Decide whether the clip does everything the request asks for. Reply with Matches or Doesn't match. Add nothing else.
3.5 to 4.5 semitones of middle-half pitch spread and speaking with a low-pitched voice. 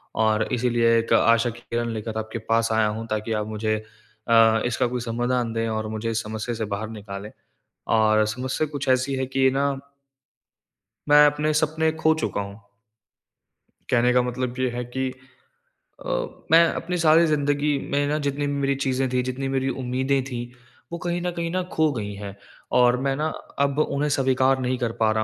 Matches